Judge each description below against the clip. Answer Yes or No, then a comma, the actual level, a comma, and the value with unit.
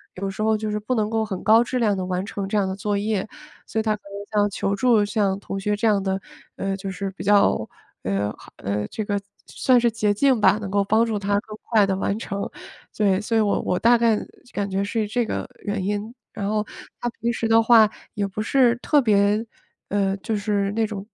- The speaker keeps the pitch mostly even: Yes, narrow, 2.0 semitones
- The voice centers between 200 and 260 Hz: Yes, high, 205 Hz